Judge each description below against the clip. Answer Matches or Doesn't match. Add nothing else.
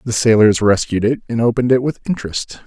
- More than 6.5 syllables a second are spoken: Doesn't match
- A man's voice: Matches